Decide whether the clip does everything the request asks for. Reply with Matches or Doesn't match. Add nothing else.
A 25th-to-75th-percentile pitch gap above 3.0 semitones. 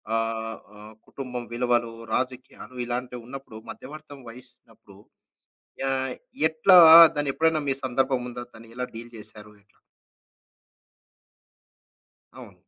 Doesn't match